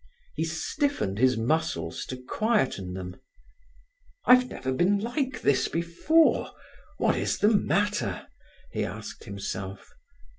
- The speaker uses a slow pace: Yes, slow, 115 wpm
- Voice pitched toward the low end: No, medium, 160 Hz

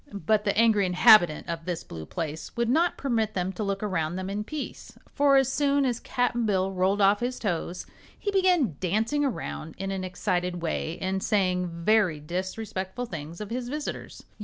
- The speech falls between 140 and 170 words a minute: No, average, 185 wpm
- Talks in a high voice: Yes, high, 195 Hz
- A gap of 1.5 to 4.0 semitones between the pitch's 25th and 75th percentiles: No, average, 5.0 semitones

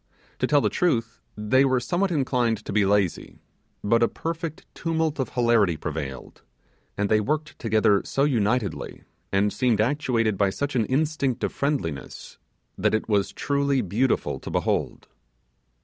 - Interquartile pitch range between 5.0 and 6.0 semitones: Yes, wide, 5.4 semitones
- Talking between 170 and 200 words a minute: No, average, 150 wpm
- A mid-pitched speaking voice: No, low, 120 Hz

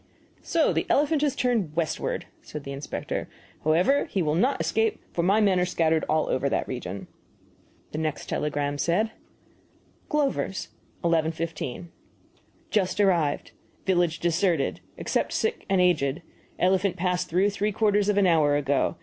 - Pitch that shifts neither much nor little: Yes, average, 4.7 semitones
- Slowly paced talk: No, average, 145 wpm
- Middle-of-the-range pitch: Yes, medium, 175 Hz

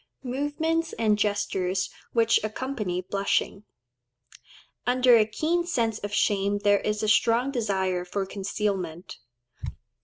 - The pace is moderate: No, slow, 110 wpm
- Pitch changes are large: No, average, 4.0 semitones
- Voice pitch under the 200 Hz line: No, high, 210 Hz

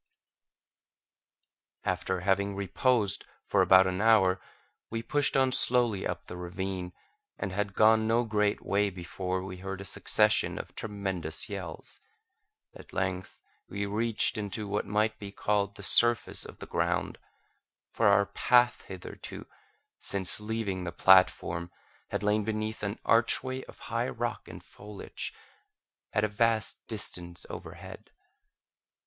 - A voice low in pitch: Yes, low, 100 Hz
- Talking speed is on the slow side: Yes, slow, 130 wpm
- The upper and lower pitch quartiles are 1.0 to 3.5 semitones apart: Yes, average, 2.8 semitones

